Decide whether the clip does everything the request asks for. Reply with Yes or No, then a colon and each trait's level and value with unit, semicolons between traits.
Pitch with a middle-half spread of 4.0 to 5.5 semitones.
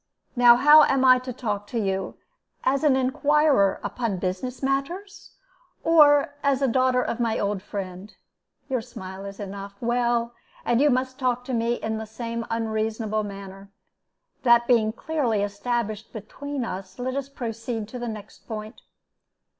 No: average, 3.6 semitones